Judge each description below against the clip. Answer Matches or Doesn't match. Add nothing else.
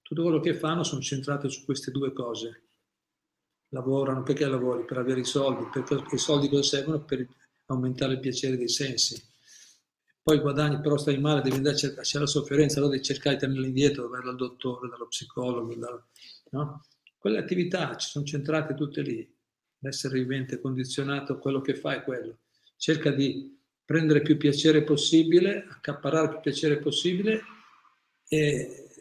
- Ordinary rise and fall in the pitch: Doesn't match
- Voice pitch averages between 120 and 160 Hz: Matches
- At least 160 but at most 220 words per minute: Matches